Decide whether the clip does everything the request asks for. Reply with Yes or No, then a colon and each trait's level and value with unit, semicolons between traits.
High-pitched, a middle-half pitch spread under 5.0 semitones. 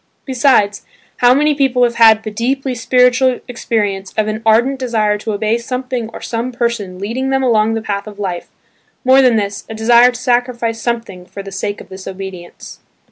Yes: high, 230 Hz; average, 3.2 semitones